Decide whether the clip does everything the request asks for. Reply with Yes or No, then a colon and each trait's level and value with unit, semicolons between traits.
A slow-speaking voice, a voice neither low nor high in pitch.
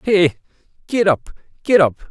Yes: slow, 115 wpm; medium, 180 Hz